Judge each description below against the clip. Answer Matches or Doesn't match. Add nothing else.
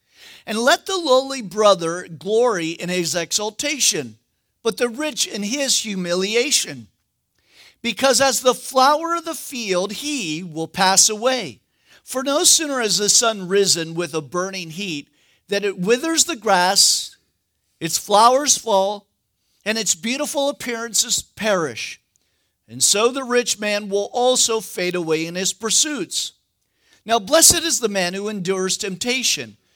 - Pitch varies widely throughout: Matches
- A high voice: Matches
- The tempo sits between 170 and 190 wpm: Doesn't match